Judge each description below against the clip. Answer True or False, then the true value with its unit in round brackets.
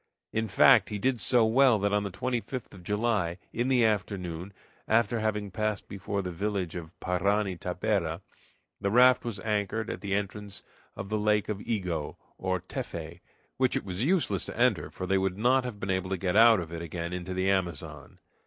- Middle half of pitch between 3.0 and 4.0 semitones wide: True (3.3 semitones)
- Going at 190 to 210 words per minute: True (195 wpm)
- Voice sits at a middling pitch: False (100 Hz)